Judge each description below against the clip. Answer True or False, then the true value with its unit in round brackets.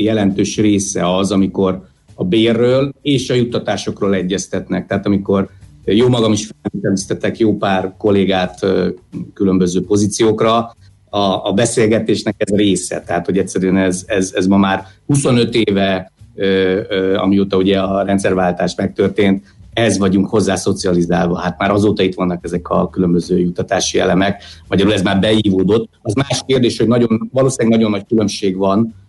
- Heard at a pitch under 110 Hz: True (100 Hz)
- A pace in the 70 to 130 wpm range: False (150 wpm)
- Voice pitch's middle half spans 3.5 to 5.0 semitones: False (2.5 semitones)